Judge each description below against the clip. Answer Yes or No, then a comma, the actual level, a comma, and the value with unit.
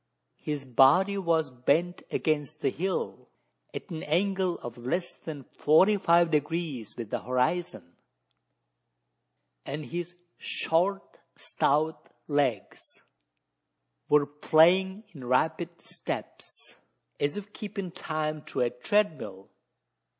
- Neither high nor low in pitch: Yes, medium, 160 Hz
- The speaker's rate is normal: No, slow, 105 wpm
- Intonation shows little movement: No, average, 4.1 semitones